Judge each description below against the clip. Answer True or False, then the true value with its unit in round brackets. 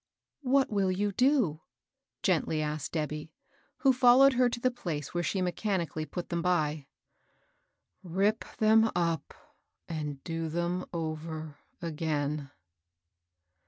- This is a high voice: False (170 Hz)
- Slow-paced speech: True (125 wpm)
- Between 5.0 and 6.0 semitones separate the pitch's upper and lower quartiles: True (5.6 semitones)